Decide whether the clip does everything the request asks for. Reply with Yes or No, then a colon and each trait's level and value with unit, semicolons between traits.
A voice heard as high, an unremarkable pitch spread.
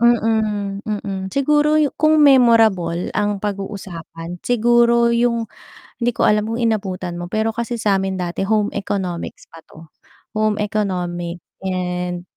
Yes: high, 205 Hz; average, 4.3 semitones